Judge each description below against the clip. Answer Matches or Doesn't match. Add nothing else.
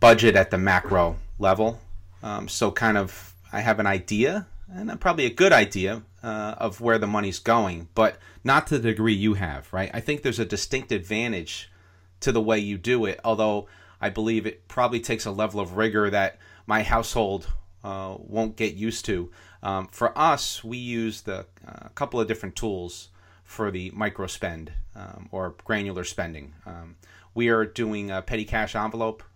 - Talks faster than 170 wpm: Matches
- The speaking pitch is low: Matches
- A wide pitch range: Doesn't match